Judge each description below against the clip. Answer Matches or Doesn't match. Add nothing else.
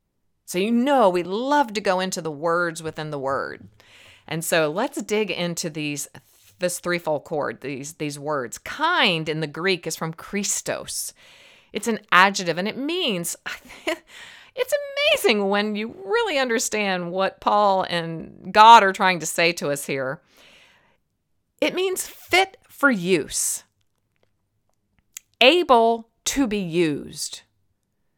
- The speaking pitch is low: Doesn't match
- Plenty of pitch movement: Matches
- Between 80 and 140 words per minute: Matches